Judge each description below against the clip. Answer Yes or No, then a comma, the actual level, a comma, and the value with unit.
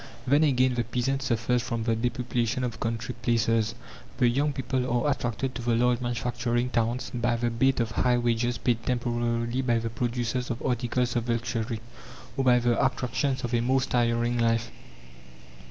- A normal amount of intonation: No, narrow, 1.3 semitones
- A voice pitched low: Yes, low, 120 Hz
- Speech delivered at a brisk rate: No, average, 170 wpm